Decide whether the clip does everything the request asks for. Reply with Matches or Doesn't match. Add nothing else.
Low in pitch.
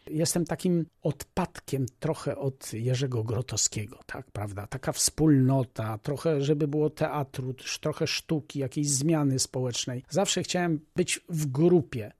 Doesn't match